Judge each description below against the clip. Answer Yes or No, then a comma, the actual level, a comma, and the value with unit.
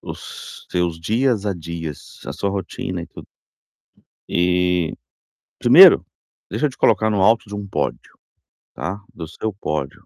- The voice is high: No, very low, 90 Hz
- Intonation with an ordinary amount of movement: Yes, average, 3.7 semitones